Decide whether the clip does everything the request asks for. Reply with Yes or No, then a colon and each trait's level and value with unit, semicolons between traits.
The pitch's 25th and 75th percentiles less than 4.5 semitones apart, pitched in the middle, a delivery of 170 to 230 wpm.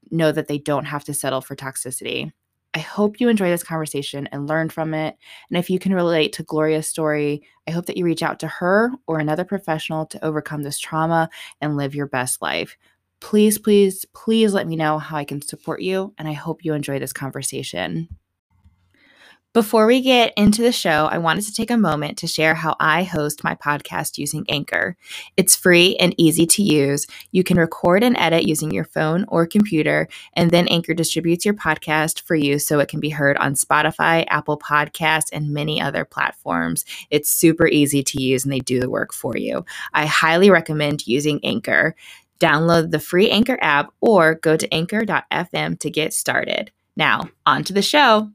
Yes: average, 3.5 semitones; medium, 160 Hz; average, 195 wpm